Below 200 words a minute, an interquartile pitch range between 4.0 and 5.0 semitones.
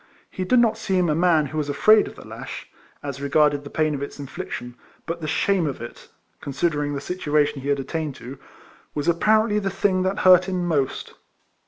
No: fast, 205 wpm; average, 4.5 semitones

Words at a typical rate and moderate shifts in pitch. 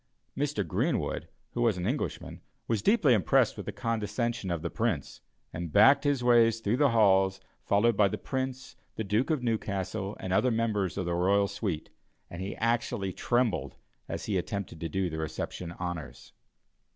Yes: average, 175 wpm; average, 4.1 semitones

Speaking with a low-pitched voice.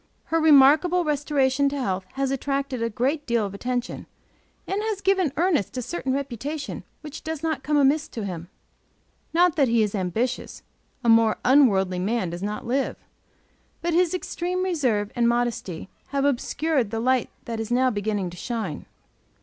No: very high, 260 Hz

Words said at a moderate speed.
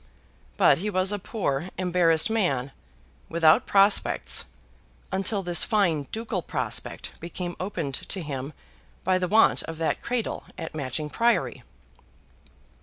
No: slow, 125 wpm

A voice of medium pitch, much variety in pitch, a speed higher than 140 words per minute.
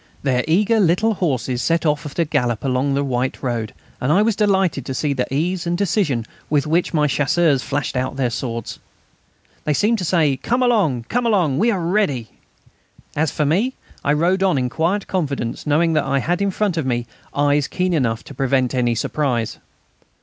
Yes: medium, 150 Hz; wide, 5.7 semitones; average, 195 wpm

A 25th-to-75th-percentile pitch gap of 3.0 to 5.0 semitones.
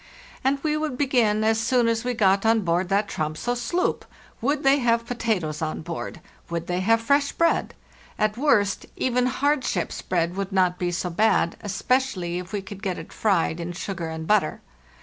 No: wide, 5.6 semitones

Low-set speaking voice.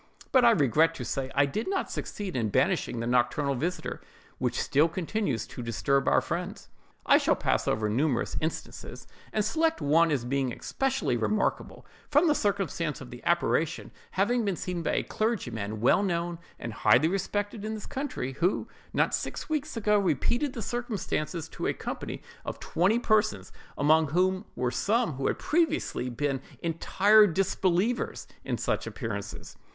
No: medium, 170 Hz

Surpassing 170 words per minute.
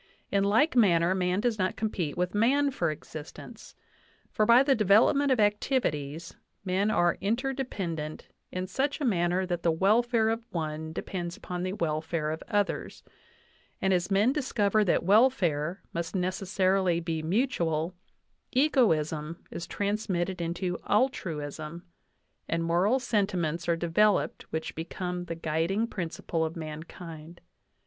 No: slow, 135 wpm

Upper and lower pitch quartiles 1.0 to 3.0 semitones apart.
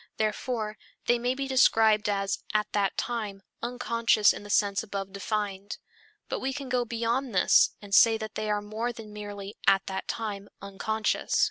Yes: narrow, 2.5 semitones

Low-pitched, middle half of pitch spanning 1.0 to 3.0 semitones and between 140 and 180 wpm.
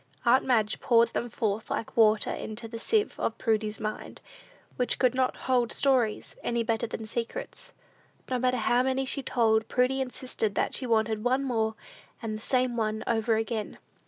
No: high, 235 Hz; narrow, 2.4 semitones; average, 175 wpm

